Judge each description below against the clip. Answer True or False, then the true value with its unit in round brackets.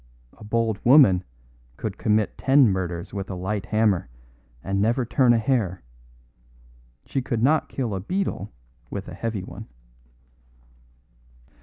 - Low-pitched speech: True (105 Hz)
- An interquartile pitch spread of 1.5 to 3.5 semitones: False (3.9 semitones)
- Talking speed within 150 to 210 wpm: False (135 wpm)